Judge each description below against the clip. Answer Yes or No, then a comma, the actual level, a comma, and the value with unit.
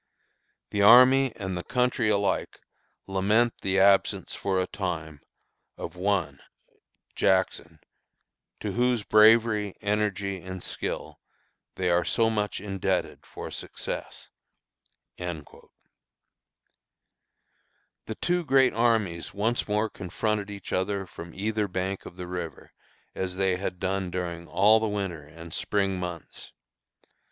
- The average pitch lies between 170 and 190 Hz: No, low, 100 Hz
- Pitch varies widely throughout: No, average, 2.9 semitones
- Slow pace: Yes, slow, 120 wpm